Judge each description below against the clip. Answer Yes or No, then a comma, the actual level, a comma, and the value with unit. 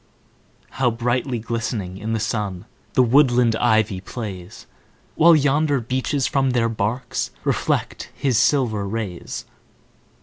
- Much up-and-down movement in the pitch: No, average, 3.6 semitones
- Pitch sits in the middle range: No, low, 115 Hz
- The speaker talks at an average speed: No, slow, 115 wpm